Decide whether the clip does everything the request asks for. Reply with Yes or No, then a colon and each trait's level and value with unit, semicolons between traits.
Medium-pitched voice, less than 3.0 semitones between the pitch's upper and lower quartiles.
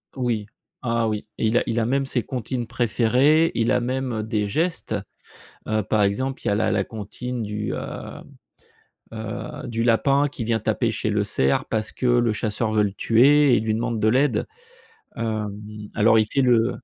No: low, 115 Hz; narrow, 2.6 semitones